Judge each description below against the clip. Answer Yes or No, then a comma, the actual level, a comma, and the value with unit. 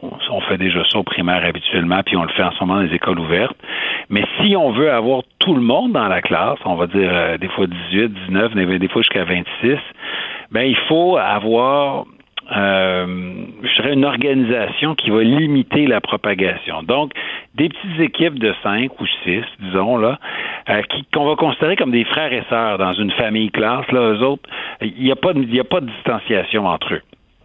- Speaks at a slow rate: No, average, 205 wpm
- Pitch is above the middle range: No, low, 115 Hz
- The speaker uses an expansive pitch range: Yes, wide, 5.9 semitones